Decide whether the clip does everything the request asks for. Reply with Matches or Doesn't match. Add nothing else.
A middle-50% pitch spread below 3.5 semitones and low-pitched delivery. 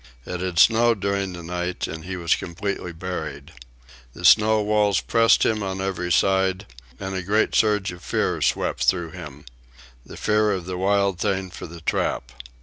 Matches